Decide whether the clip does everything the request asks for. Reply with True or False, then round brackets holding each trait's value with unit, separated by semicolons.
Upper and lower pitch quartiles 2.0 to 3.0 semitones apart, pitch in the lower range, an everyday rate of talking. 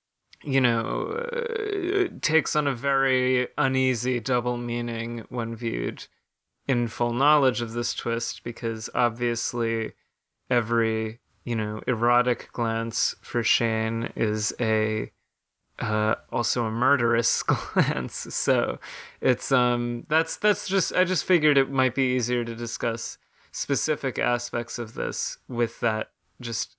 False (2.6 semitones; 120 Hz; 125 wpm)